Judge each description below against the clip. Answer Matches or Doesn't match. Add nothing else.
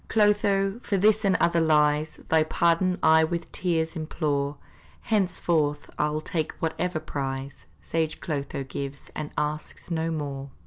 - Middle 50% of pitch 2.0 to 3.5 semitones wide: Matches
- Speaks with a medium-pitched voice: Matches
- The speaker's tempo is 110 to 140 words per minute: Matches